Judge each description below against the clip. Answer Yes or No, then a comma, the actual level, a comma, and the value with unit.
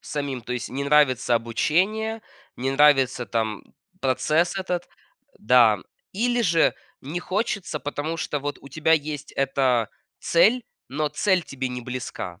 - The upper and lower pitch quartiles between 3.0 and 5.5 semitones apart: Yes, average, 5.1 semitones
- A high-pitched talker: No, medium, 145 Hz